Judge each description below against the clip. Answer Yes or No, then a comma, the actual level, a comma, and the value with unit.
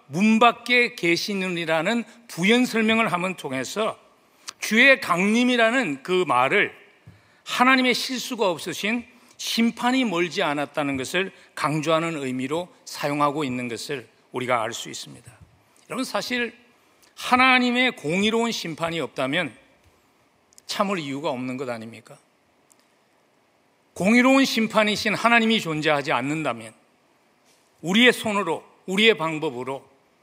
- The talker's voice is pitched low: No, high, 190 Hz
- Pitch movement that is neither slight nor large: No, wide, 7.4 semitones